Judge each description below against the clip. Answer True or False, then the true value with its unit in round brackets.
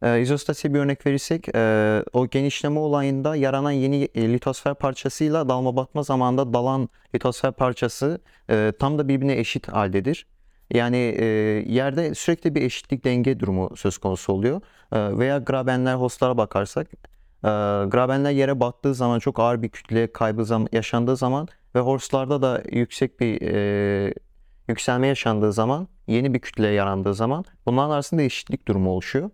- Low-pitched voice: True (125 Hz)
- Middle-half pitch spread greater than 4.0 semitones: False (3.6 semitones)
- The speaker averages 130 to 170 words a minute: True (135 wpm)